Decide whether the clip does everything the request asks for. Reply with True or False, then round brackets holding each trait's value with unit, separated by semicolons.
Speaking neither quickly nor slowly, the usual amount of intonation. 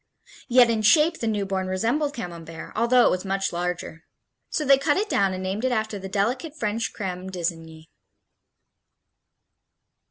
True (155 wpm; 5.0 semitones)